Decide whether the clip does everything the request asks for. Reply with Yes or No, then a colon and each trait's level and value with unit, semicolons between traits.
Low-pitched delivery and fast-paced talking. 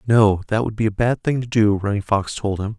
Yes: low, 105 Hz; fast, 280 wpm